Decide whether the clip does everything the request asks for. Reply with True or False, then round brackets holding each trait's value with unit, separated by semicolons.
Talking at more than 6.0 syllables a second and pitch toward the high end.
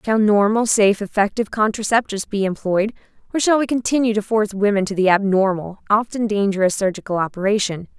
True (6.2 syllables/s; 205 Hz)